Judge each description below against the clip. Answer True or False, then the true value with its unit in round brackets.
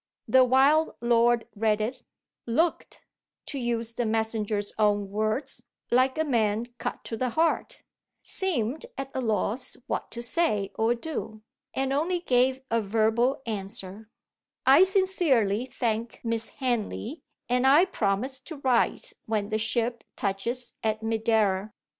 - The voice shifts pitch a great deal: False (3.5 semitones)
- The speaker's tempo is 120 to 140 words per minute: True (135 wpm)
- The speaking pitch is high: True (235 Hz)